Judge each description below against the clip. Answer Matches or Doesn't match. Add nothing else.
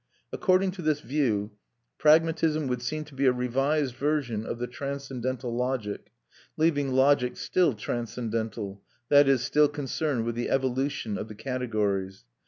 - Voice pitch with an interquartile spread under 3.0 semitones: Doesn't match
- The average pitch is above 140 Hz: Doesn't match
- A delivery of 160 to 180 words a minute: Doesn't match